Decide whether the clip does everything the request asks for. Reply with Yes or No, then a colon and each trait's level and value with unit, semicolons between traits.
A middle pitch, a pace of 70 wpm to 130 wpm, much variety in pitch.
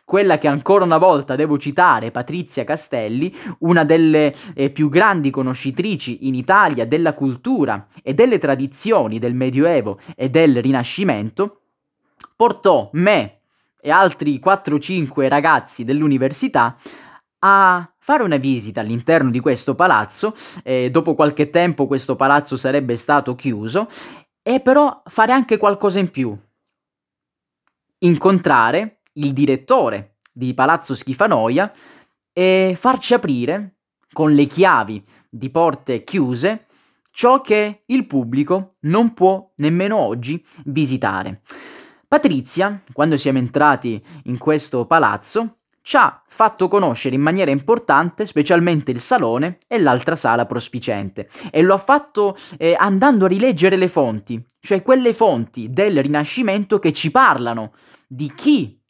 Yes: medium, 155 Hz; average, 125 wpm; wide, 6.6 semitones